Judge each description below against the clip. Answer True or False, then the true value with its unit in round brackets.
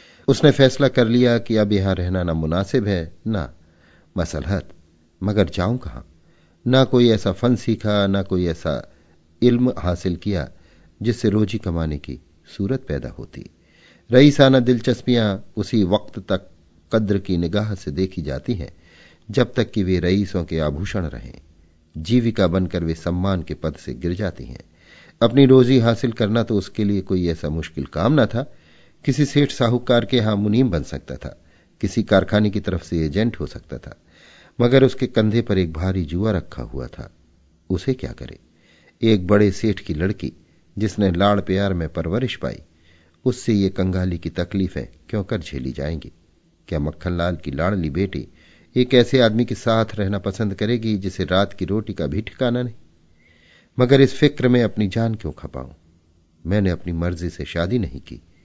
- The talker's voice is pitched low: True (95 Hz)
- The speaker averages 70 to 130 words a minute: False (165 wpm)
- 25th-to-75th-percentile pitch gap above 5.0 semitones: True (5.4 semitones)